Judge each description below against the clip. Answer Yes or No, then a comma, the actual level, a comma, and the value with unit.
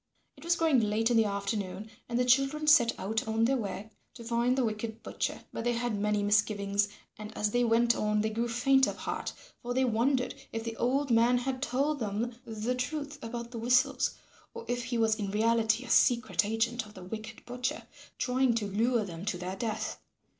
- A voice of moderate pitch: No, high, 230 Hz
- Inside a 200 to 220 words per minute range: Yes, fast, 205 wpm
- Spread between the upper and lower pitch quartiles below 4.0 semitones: Yes, narrow, 2.6 semitones